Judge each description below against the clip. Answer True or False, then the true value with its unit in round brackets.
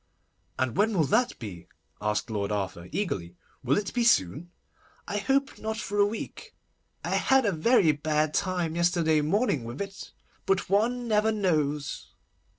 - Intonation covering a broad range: True (7.1 semitones)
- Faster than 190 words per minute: False (155 wpm)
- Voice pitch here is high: False (175 Hz)